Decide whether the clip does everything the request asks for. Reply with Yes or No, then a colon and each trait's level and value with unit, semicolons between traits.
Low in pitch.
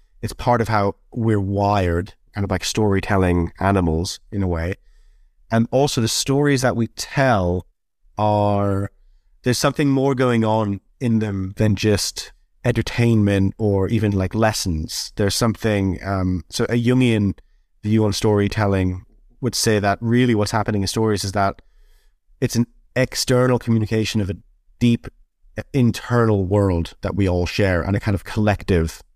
Yes: low, 105 Hz